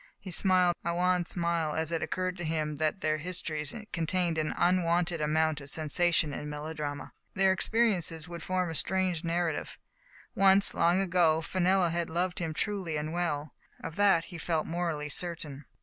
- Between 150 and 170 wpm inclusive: Yes, average, 165 wpm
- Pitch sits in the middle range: Yes, medium, 170 Hz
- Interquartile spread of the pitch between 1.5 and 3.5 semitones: Yes, narrow, 2.5 semitones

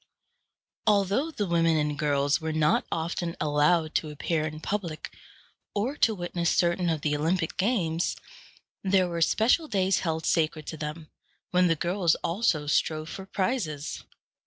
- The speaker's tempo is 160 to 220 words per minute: No, average, 150 wpm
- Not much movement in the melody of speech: No, average, 3.4 semitones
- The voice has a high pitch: No, medium, 170 Hz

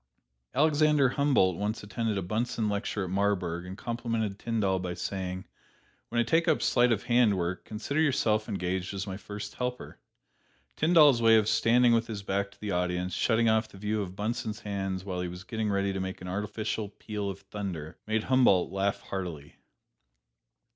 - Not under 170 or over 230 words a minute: Yes, average, 180 wpm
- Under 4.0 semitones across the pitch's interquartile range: Yes, average, 3.5 semitones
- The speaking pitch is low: Yes, low, 105 Hz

